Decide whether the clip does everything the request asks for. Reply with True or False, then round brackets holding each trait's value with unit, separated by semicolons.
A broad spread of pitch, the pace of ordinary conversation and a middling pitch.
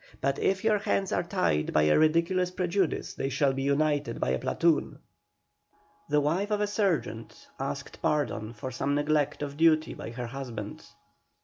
False (4.7 semitones; 170 wpm; 150 Hz)